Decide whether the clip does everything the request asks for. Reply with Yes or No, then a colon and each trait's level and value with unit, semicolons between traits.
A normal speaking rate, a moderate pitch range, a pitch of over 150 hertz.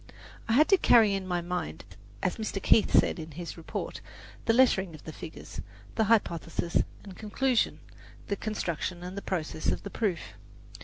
Yes: average, 170 wpm; average, 4.4 semitones; high, 190 Hz